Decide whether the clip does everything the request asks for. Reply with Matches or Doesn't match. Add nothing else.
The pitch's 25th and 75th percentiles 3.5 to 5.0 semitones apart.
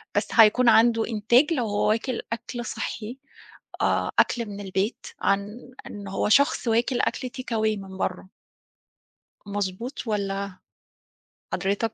Doesn't match